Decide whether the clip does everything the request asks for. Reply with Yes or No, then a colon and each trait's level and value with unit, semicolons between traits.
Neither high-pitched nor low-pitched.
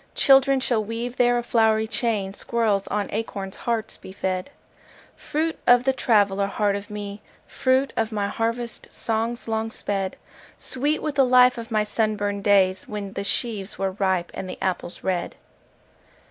No: high, 220 Hz